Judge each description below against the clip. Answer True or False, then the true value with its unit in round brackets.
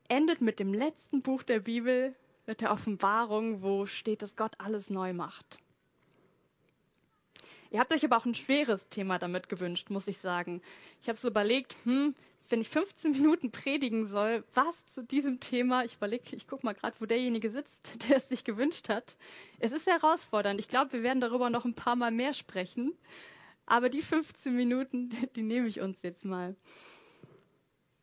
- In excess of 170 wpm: True (180 wpm)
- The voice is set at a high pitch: True (235 Hz)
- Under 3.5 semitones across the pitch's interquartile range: False (4.3 semitones)